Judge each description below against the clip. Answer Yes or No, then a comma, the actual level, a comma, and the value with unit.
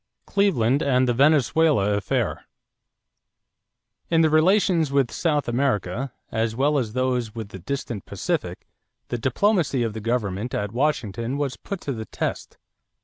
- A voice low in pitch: Yes, low, 130 Hz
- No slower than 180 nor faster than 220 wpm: No, average, 145 wpm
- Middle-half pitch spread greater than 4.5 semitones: Yes, average, 4.9 semitones